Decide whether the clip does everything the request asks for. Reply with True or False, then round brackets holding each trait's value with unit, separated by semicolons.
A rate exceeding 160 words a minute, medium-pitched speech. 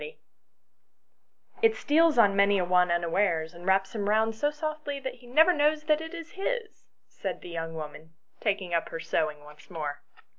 False (185 wpm; 205 Hz)